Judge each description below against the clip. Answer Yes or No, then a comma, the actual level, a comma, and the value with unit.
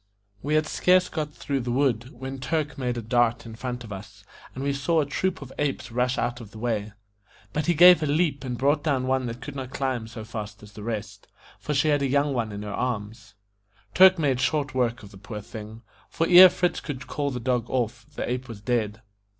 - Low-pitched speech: Yes, low, 125 Hz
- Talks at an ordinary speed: No, fast, 230 wpm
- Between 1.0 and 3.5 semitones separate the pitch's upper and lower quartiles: No, average, 4.2 semitones